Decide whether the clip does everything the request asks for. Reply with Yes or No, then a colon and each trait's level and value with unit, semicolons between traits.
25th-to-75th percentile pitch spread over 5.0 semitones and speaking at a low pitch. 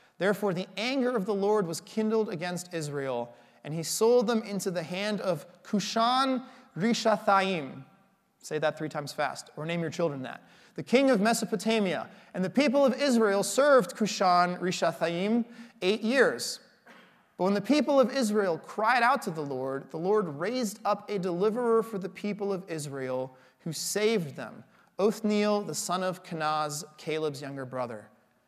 No: wide, 5.4 semitones; high, 195 Hz